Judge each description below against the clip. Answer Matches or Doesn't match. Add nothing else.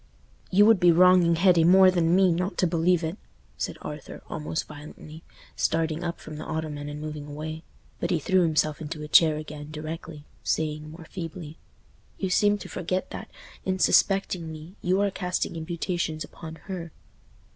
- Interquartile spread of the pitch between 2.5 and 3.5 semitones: Matches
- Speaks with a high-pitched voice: Doesn't match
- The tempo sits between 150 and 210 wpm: Matches